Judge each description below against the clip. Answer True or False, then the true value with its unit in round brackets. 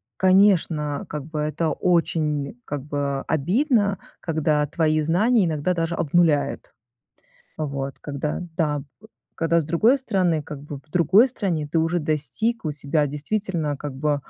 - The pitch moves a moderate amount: True (3.3 semitones)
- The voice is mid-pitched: True (155 Hz)